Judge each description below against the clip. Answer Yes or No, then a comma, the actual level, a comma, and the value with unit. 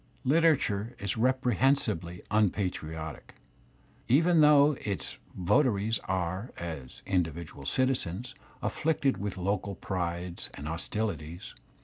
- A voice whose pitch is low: Yes, low, 100 Hz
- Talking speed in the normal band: No, slow, 95 wpm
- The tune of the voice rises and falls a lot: Yes, wide, 6.9 semitones